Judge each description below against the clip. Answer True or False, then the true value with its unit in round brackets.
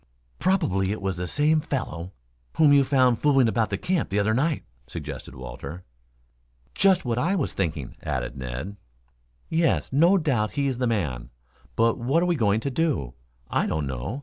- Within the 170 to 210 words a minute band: True (175 wpm)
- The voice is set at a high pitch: False (115 Hz)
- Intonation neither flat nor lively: False (8.3 semitones)